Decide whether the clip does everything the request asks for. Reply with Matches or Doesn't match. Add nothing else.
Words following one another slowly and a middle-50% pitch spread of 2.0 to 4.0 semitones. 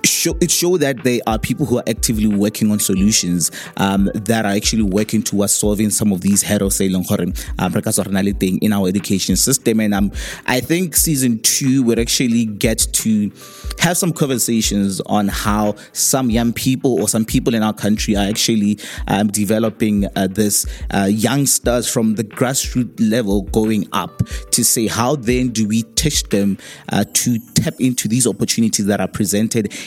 Doesn't match